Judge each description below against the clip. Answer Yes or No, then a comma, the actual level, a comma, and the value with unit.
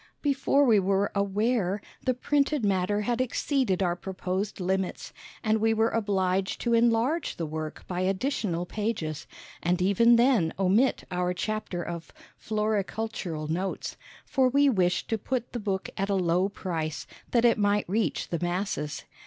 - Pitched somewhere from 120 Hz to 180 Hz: No, high, 200 Hz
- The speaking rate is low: No, average, 155 wpm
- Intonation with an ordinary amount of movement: Yes, average, 4.2 semitones